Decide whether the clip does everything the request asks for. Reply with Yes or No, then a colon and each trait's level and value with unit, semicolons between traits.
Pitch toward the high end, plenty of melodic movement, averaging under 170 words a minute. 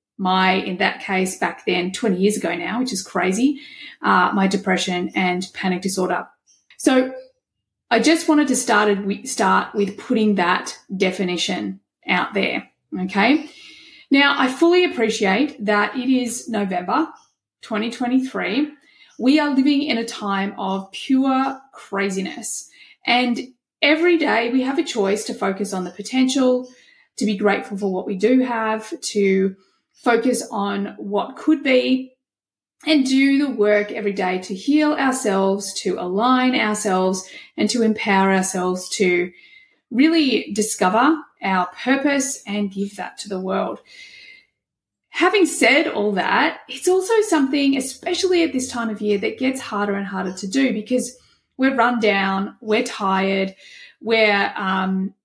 Yes: high, 230 Hz; wide, 6.1 semitones; average, 145 wpm